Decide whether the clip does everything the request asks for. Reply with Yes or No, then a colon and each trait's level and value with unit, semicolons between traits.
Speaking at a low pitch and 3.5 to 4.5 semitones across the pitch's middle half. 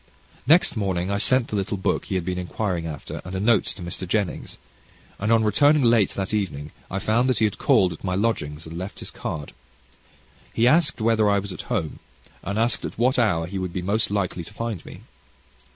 Yes: low, 100 Hz; average, 3.8 semitones